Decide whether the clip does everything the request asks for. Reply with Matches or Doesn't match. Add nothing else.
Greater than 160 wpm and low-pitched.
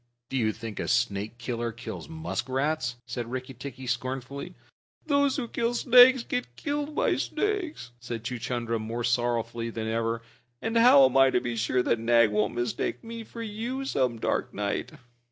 Matches